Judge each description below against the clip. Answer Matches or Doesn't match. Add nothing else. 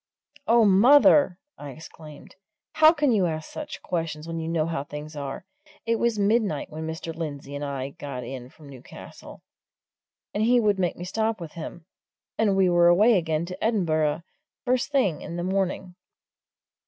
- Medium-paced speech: Matches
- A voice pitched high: Doesn't match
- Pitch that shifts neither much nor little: Doesn't match